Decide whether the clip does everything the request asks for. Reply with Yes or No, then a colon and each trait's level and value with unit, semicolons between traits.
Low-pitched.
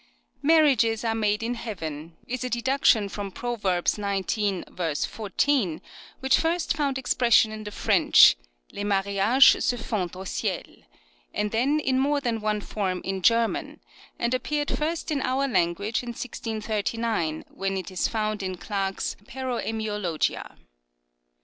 No: high, 220 Hz